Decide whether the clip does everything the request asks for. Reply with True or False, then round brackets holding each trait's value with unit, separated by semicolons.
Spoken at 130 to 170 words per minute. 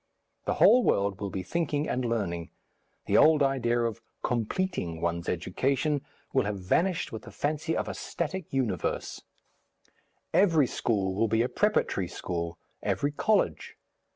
True (145 wpm)